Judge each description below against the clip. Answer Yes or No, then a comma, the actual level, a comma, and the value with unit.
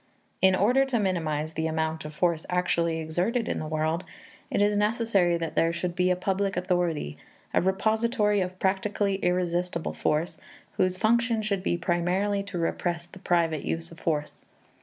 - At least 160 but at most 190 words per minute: Yes, average, 165 wpm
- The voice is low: No, medium, 180 Hz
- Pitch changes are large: No, average, 3.2 semitones